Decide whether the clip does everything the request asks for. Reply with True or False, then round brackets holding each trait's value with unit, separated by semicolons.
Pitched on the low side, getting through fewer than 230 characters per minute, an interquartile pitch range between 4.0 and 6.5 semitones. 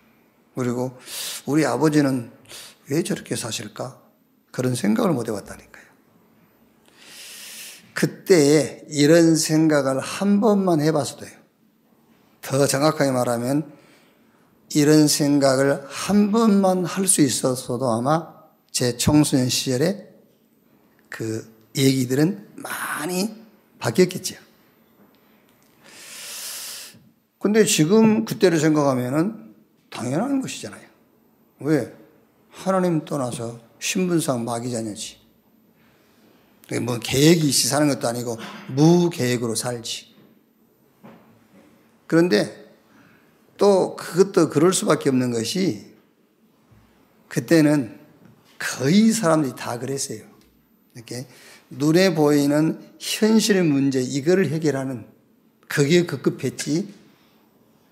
False (145 Hz; 205 characters per minute; 5.8 semitones)